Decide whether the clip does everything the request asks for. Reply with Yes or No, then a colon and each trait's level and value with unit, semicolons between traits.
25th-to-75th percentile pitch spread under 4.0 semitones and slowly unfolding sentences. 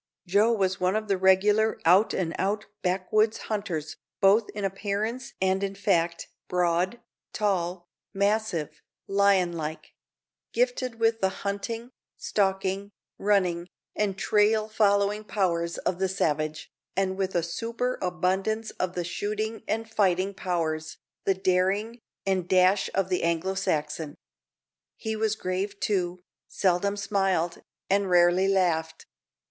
Yes: average, 2.7 semitones; slow, 125 wpm